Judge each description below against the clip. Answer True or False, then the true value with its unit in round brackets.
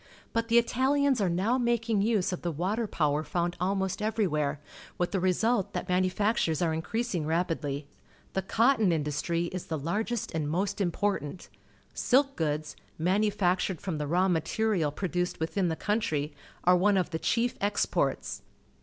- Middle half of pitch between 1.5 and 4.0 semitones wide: False (4.7 semitones)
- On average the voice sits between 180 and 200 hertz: True (185 Hz)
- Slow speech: False (155 wpm)